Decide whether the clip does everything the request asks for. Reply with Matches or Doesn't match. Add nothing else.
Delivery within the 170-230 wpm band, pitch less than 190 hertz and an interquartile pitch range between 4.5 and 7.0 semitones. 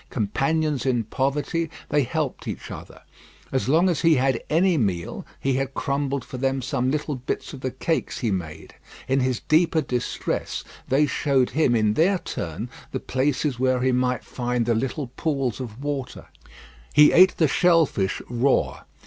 Doesn't match